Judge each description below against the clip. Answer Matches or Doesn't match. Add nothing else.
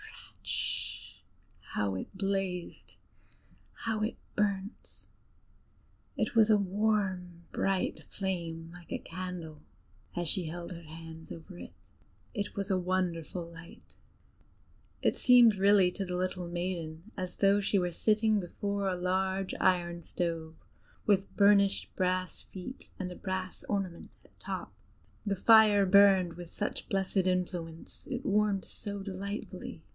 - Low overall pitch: Doesn't match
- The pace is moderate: Doesn't match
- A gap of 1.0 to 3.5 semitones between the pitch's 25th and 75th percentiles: Matches